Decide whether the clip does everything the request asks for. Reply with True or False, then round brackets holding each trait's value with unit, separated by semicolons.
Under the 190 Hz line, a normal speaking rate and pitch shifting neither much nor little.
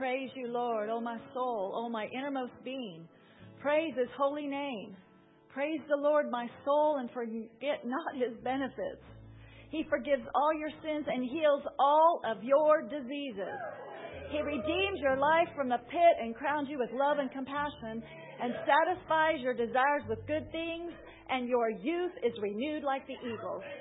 False (275 Hz; 165 wpm; 3.8 semitones)